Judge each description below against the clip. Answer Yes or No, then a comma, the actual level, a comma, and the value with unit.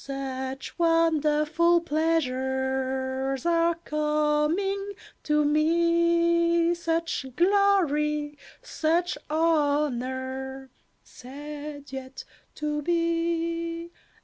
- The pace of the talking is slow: Yes, slow, 65 wpm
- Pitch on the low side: No, very high, 305 Hz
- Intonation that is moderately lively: Yes, average, 3.6 semitones